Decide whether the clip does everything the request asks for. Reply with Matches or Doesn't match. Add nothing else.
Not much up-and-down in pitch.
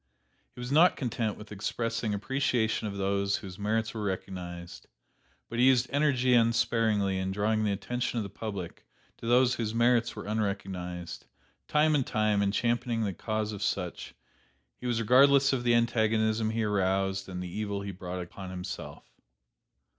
Doesn't match